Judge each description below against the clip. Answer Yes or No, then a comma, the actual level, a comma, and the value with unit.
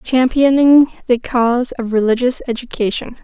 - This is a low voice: No, high, 245 Hz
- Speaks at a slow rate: Yes, slow, 110 wpm